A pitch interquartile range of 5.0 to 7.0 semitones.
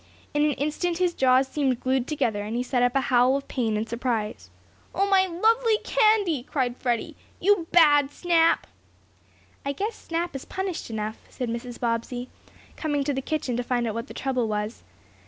Yes: wide, 5.6 semitones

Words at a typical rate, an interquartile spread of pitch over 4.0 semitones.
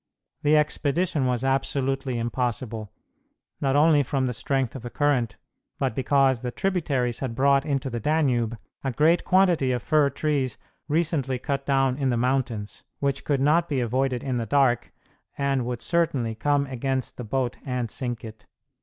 No: average, 165 wpm; average, 2.8 semitones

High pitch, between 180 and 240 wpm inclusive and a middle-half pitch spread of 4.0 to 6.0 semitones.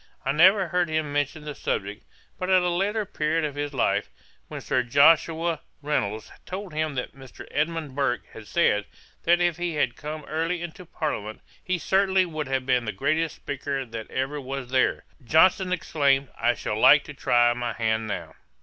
No: medium, 150 Hz; average, 185 wpm; average, 4.6 semitones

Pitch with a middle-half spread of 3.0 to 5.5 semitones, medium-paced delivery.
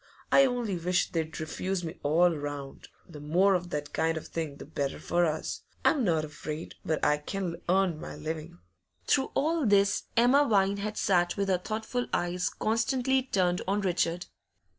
Yes: average, 4.4 semitones; average, 175 wpm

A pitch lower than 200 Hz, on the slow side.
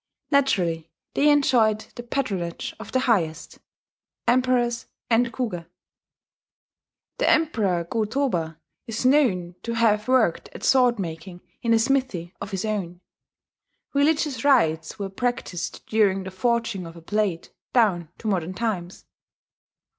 No: high, 215 Hz; slow, 130 wpm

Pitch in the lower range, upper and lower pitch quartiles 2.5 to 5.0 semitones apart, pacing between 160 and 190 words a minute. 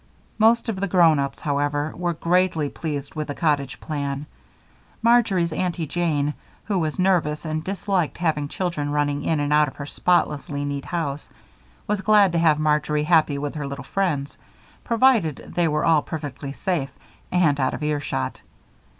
No: medium, 155 Hz; average, 3.5 semitones; average, 165 wpm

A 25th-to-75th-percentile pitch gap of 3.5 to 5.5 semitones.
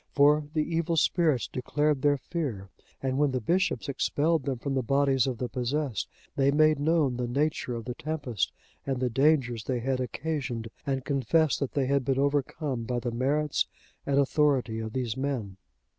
No: average, 3.1 semitones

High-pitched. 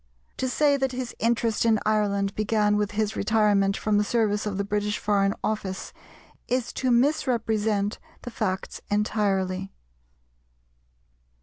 Yes: high, 210 Hz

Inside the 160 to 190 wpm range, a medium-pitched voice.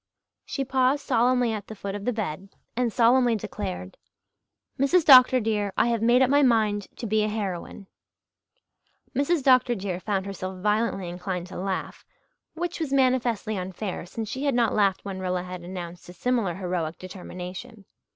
No: average, 170 wpm; high, 210 Hz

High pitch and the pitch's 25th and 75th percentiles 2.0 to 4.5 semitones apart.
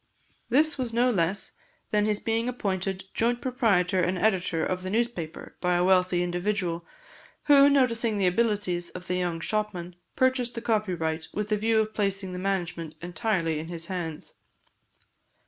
Yes: high, 195 Hz; average, 4.2 semitones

